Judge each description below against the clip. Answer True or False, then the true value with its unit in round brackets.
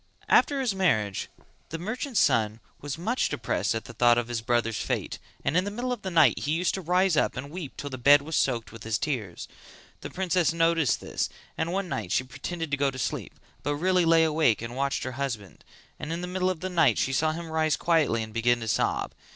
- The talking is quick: True (230 wpm)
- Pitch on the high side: False (150 Hz)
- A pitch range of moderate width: False (6.7 semitones)